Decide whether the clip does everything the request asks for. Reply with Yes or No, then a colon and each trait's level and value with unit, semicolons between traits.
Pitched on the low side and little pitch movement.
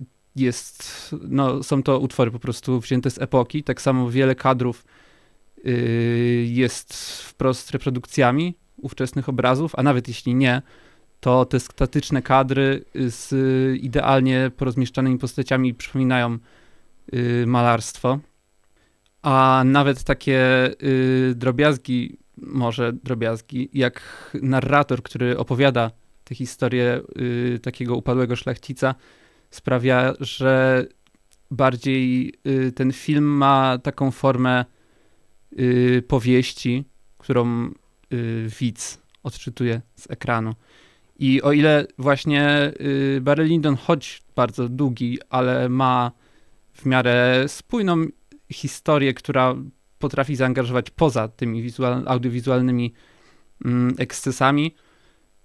Yes: low, 130 Hz; narrow, 1.7 semitones